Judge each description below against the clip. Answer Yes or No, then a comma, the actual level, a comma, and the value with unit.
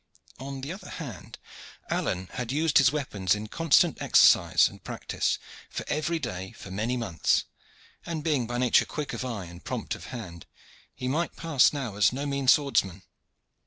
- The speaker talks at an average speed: Yes, average, 170 wpm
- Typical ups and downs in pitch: No, wide, 6.0 semitones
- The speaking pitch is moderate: No, low, 125 Hz